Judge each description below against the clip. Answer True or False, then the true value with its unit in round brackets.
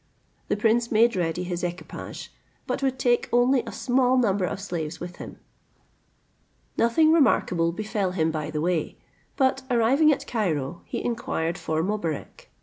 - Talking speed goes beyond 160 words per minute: False (150 wpm)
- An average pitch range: False (6.1 semitones)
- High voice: True (205 Hz)